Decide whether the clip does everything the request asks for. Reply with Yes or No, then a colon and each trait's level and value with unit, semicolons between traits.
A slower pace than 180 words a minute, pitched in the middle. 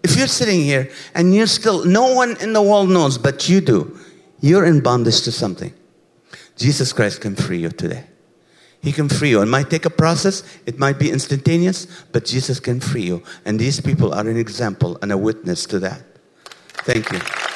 No: average, 200 wpm; medium, 150 Hz